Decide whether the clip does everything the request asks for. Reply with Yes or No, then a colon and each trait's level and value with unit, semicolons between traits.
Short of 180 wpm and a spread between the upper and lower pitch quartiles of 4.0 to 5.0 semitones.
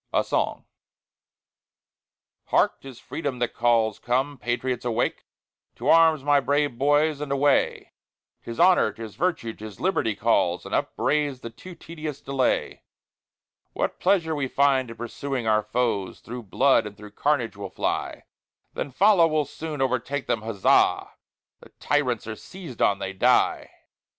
Yes: average, 145 wpm; average, 4.4 semitones